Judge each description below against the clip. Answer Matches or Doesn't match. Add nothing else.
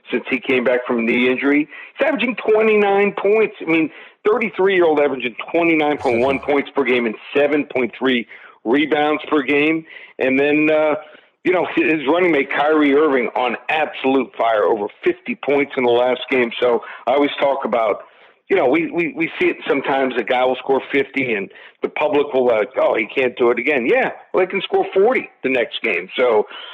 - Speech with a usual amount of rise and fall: Doesn't match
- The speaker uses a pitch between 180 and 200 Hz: Doesn't match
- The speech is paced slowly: Doesn't match